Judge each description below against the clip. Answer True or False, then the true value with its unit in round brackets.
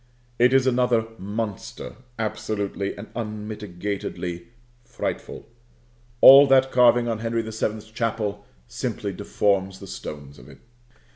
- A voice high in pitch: False (110 Hz)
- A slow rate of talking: True (120 wpm)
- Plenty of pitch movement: False (3.0 semitones)